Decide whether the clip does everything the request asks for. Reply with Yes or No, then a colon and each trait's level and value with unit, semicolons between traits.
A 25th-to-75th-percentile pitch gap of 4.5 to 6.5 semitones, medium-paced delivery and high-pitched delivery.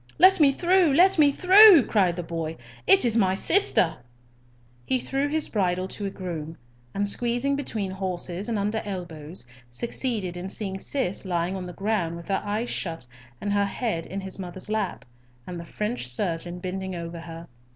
Yes: average, 5.2 semitones; average, 180 wpm; high, 195 Hz